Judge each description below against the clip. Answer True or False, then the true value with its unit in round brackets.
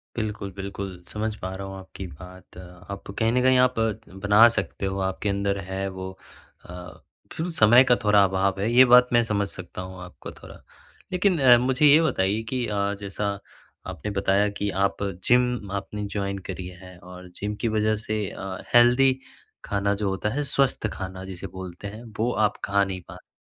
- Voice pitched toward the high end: False (100 Hz)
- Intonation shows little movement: False (3.3 semitones)